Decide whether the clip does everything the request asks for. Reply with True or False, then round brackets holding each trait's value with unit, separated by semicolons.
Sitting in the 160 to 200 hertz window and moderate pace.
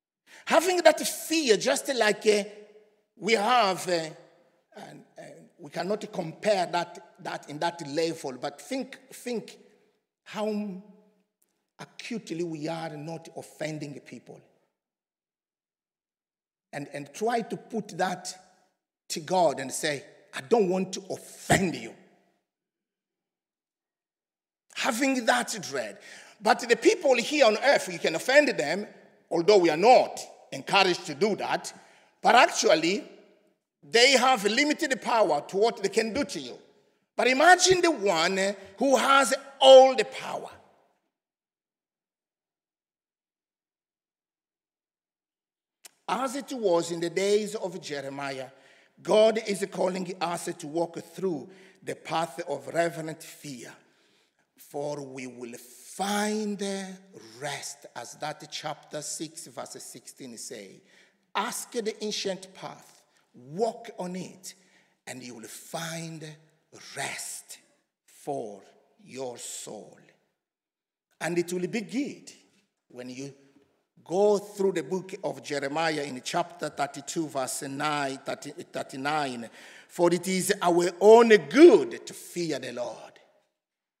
False (185 Hz; 120 wpm)